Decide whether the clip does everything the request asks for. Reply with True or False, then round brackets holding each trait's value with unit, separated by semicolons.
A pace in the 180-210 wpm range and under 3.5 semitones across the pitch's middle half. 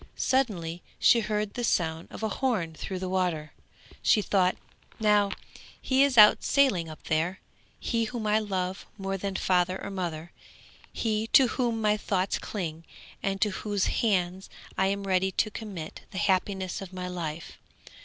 False (165 wpm; 3.0 semitones)